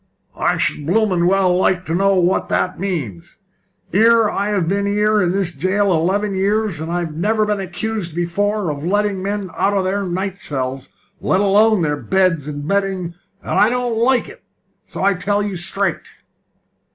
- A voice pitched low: No, high, 195 Hz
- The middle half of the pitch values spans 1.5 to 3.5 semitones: Yes, average, 2.9 semitones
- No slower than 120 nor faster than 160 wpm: No, average, 175 wpm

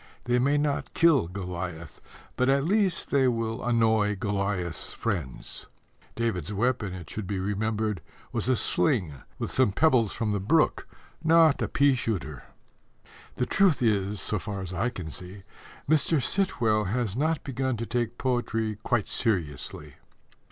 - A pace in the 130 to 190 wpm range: Yes, average, 150 wpm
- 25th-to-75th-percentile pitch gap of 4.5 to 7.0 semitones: Yes, average, 5.1 semitones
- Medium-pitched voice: No, low, 110 Hz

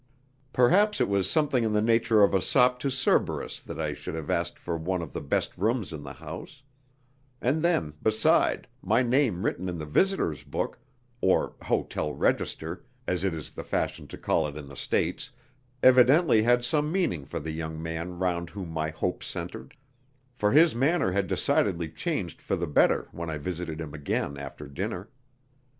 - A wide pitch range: Yes, wide, 7.5 semitones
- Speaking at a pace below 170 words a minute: No, average, 185 wpm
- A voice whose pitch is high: No, very low, 90 Hz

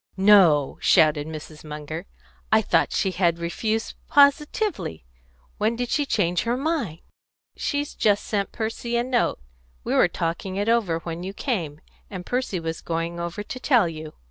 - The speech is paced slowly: No, average, 160 wpm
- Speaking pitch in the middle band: No, high, 195 Hz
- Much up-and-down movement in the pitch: Yes, wide, 6.1 semitones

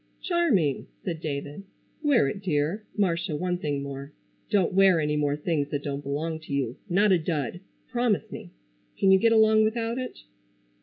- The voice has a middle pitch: Yes, medium, 170 Hz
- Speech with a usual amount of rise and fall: No, wide, 6.1 semitones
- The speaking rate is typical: Yes, average, 170 wpm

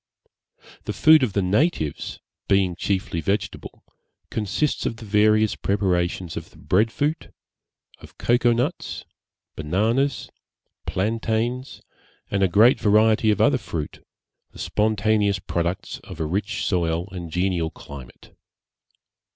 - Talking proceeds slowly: Yes, slow, 120 wpm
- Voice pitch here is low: Yes, low, 100 Hz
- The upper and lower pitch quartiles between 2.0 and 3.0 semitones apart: No, average, 4.0 semitones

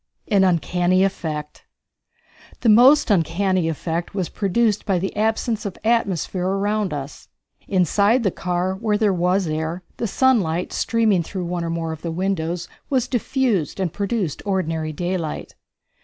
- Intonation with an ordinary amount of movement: Yes, average, 3.7 semitones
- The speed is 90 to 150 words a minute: Yes, average, 145 wpm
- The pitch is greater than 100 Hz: Yes, medium, 185 Hz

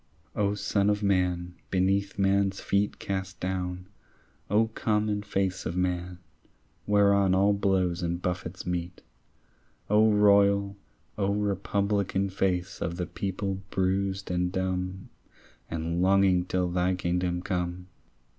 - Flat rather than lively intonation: Yes, narrow, 1.8 semitones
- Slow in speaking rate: Yes, slow, 120 wpm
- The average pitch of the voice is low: Yes, very low, 95 Hz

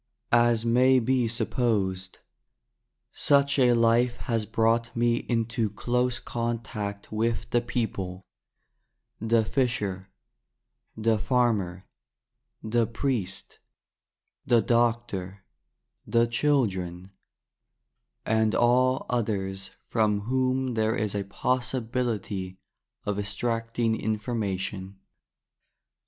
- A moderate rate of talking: No, slow, 90 wpm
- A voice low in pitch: Yes, low, 115 Hz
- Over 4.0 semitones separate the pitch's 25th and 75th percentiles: No, average, 2.9 semitones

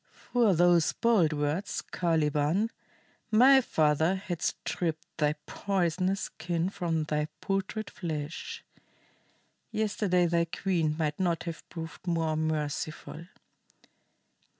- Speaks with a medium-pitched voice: Yes, medium, 170 Hz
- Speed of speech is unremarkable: No, slow, 105 wpm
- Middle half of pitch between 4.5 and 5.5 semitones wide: No, average, 3.5 semitones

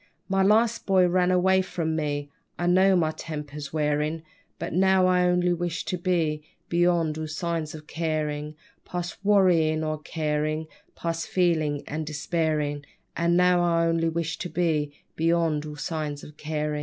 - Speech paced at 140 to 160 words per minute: Yes, average, 155 wpm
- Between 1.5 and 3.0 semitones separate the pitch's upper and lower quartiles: Yes, average, 2.7 semitones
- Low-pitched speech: No, medium, 165 Hz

